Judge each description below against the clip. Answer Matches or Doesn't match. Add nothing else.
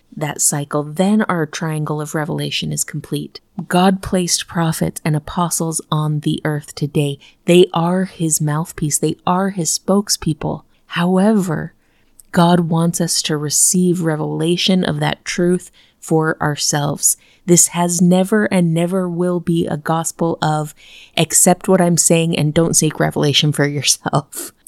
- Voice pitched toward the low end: Doesn't match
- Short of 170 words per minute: Matches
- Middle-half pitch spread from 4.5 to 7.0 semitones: Doesn't match